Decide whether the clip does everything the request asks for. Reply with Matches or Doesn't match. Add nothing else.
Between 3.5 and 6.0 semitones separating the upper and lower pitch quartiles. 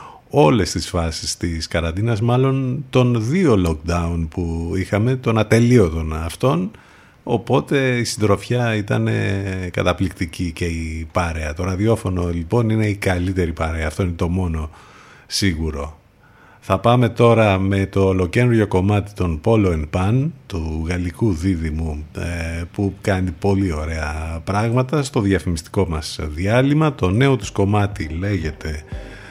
Matches